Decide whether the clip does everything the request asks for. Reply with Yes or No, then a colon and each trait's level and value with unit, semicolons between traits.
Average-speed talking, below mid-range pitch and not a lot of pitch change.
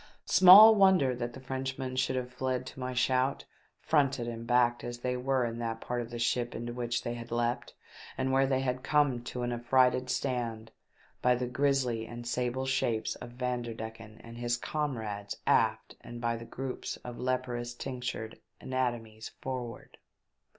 Yes: average, 170 wpm; low, 125 Hz; narrow, 1.6 semitones